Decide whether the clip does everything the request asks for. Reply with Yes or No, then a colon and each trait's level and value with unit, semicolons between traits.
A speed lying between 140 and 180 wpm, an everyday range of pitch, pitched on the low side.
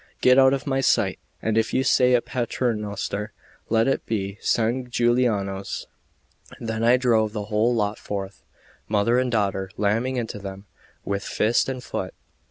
Yes: average, 160 wpm; average, 3.3 semitones; low, 115 Hz